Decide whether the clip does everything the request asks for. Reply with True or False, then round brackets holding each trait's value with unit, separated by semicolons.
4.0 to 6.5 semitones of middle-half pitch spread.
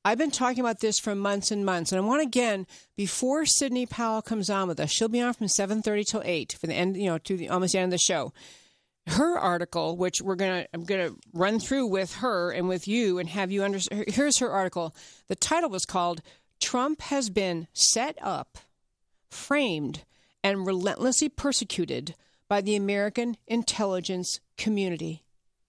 True (4.3 semitones)